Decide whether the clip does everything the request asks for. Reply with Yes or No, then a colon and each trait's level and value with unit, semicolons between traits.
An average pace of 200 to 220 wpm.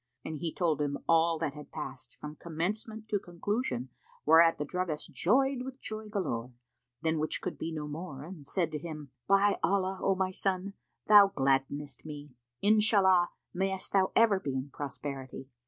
No: average, 170 wpm